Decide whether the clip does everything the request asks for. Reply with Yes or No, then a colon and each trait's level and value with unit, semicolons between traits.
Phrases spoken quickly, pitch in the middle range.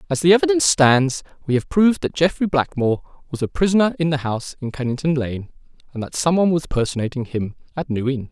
Yes: fast, 210 wpm; medium, 145 Hz